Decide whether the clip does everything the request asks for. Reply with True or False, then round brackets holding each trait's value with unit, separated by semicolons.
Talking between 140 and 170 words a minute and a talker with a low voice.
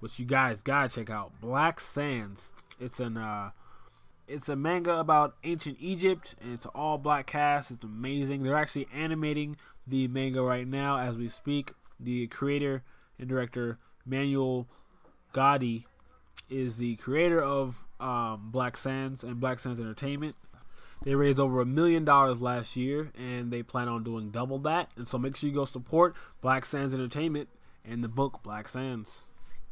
True (160 wpm; 130 Hz)